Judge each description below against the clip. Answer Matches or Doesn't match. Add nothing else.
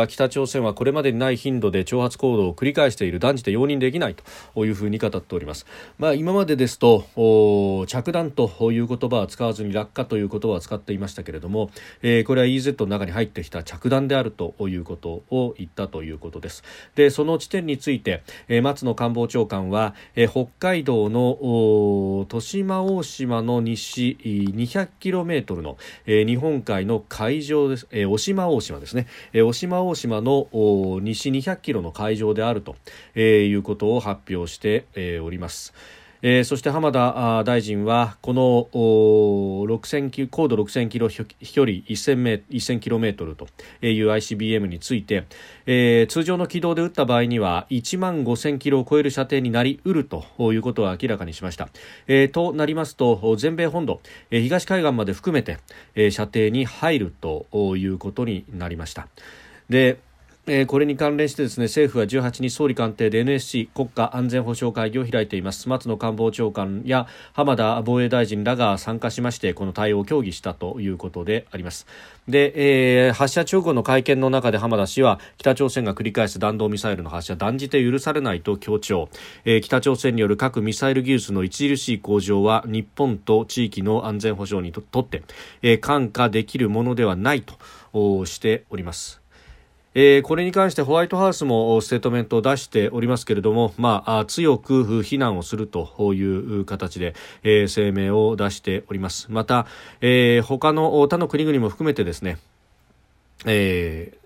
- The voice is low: Matches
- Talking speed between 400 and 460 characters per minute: Doesn't match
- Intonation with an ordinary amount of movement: Matches